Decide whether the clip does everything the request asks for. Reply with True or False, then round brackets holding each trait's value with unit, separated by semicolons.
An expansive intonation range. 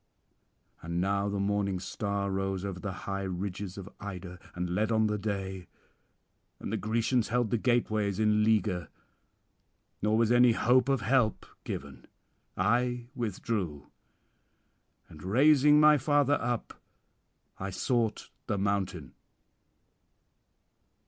False (3.7 semitones)